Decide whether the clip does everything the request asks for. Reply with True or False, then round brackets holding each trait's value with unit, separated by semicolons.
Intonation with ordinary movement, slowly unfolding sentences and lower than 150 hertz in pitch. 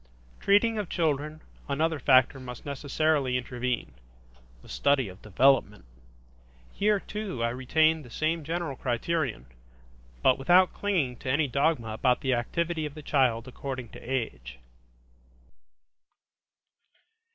True (4.3 semitones; 120 wpm; 140 Hz)